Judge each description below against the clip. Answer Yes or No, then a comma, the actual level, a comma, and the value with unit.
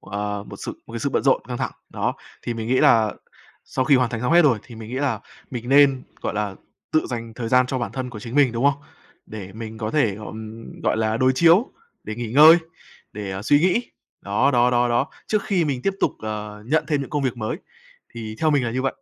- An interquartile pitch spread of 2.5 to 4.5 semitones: Yes, average, 4.2 semitones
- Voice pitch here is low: Yes, low, 120 Hz